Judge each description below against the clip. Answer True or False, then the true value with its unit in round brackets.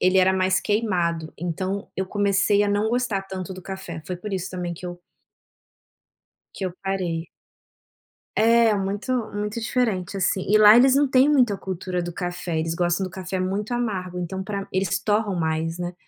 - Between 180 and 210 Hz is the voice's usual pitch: True (190 Hz)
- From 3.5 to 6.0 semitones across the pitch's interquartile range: False (2.7 semitones)